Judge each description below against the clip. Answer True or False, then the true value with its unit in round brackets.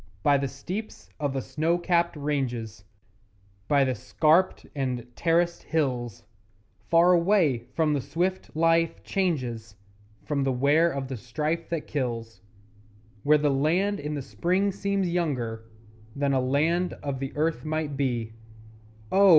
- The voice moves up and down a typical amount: True (4.4 semitones)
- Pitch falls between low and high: True (150 Hz)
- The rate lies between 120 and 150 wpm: True (140 wpm)